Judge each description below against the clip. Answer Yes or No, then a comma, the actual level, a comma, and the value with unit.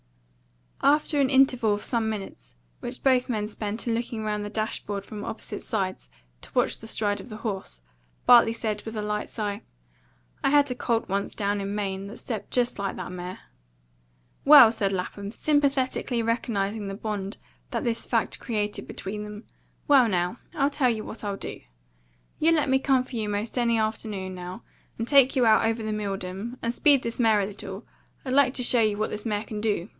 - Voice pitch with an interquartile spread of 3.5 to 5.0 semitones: No, average, 3.1 semitones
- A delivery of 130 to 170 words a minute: No, average, 200 wpm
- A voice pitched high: Yes, high, 220 Hz